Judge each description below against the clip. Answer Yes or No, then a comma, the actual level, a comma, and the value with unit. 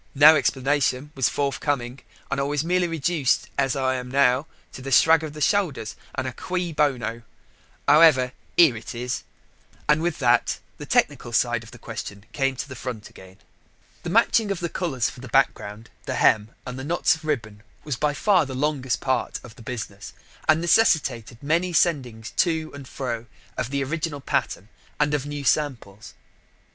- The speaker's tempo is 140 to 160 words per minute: No, average, 180 wpm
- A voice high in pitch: No, low, 135 Hz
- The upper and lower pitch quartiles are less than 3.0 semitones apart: No, average, 4.0 semitones